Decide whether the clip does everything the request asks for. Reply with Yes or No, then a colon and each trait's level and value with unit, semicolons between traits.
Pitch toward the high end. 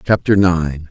No: very low, 85 Hz